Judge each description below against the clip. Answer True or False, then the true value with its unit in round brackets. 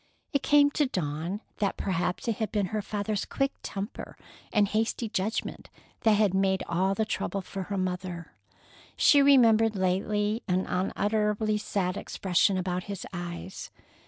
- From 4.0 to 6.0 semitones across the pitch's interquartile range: False (2.8 semitones)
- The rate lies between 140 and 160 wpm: True (150 wpm)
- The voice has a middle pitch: False (200 Hz)